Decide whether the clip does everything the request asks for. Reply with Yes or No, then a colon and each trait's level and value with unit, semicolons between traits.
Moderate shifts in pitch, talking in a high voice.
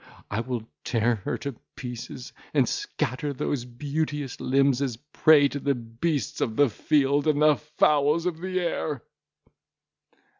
No: average, 3.6 semitones; medium, 140 Hz